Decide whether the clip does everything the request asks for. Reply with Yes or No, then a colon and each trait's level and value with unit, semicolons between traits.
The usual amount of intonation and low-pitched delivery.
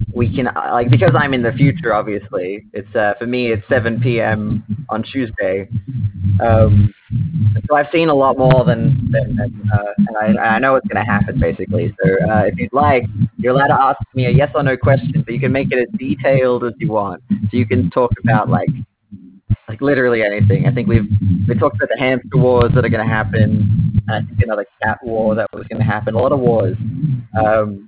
Yes: average, 3.3 semitones; low, 115 Hz